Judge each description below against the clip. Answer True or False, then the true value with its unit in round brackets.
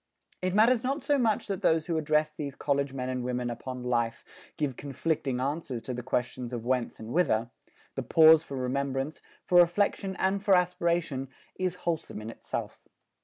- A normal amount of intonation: False (5.8 semitones)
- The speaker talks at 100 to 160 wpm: False (175 wpm)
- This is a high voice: False (145 Hz)